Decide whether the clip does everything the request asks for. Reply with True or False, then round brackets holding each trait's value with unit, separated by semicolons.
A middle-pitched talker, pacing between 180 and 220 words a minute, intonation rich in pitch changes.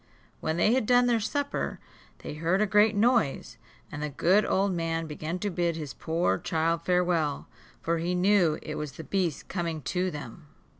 False (170 Hz; 185 wpm; 4.1 semitones)